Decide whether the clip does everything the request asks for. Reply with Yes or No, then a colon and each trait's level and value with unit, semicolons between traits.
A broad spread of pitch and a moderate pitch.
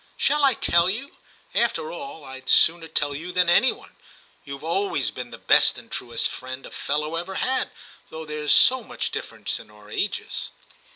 Yes: wide, 6.5 semitones; medium, 160 Hz